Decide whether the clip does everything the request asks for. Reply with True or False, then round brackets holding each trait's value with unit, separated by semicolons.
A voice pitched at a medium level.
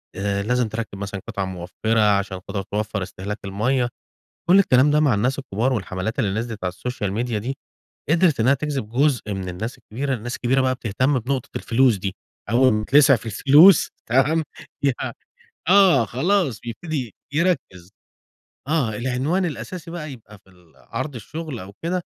False (120 Hz)